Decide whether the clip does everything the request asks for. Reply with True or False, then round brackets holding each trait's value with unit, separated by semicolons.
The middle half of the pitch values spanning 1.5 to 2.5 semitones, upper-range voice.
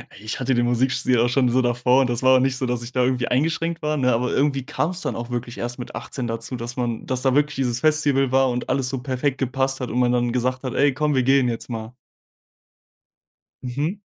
False (1.8 semitones; 130 Hz)